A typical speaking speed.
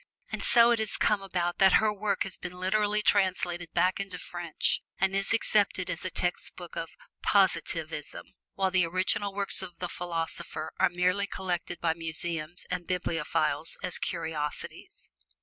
Yes: average, 155 wpm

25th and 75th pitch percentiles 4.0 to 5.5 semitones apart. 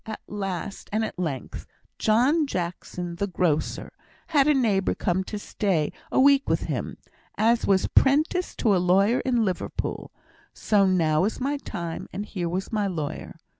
Yes: average, 5.0 semitones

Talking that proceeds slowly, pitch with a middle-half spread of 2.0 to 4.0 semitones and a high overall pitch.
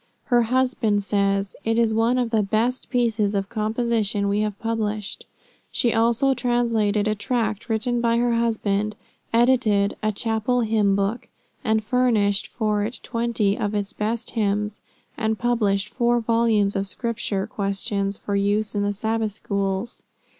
No: average, 150 wpm; narrow, 2.4 semitones; high, 220 Hz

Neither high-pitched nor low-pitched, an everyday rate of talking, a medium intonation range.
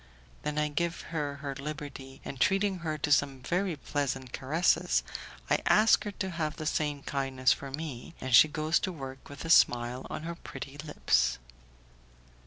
Yes: medium, 145 Hz; average, 175 wpm; average, 3.3 semitones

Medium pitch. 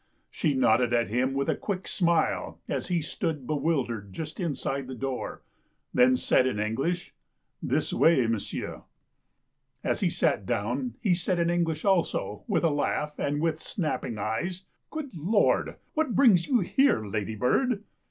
Yes: medium, 150 Hz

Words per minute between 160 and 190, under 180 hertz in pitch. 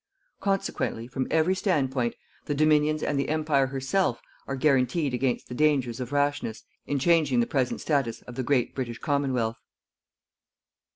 No: average, 150 wpm; low, 135 Hz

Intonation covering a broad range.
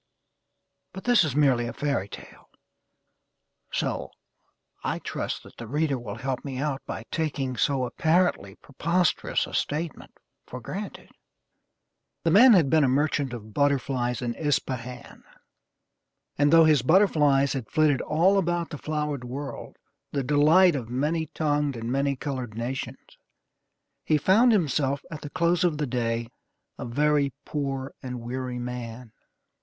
No: average, 3.8 semitones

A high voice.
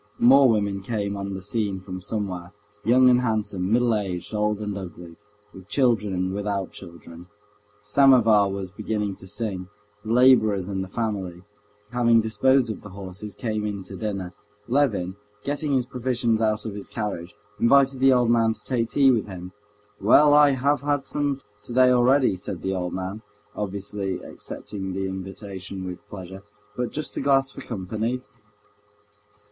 No: low, 105 Hz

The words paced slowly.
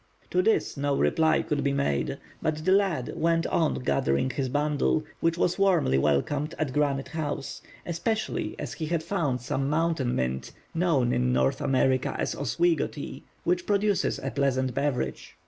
No: average, 165 wpm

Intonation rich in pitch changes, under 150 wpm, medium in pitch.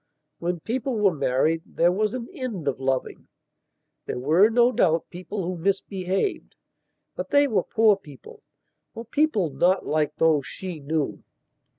Yes: wide, 5.7 semitones; slow, 135 wpm; medium, 180 Hz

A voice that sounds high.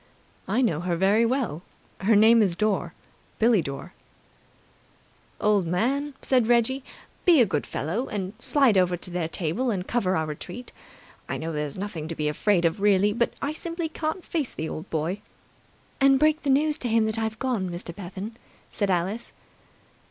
Yes: high, 210 Hz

